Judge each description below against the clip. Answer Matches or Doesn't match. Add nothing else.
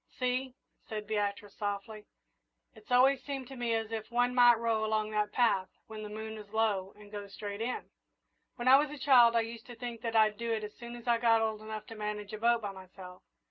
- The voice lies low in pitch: Doesn't match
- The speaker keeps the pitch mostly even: Matches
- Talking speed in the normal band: Doesn't match